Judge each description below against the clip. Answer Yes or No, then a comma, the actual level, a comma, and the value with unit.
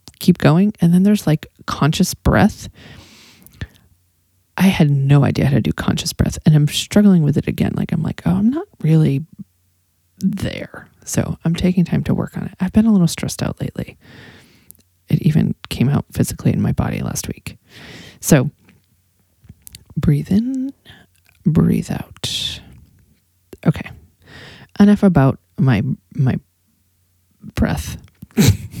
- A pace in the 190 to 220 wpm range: No, average, 140 wpm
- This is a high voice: No, medium, 140 Hz